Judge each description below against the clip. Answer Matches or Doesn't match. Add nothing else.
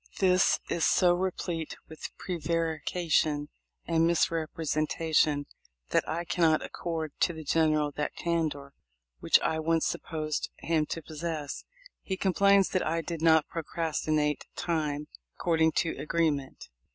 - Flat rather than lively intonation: Matches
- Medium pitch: Matches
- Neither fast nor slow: Doesn't match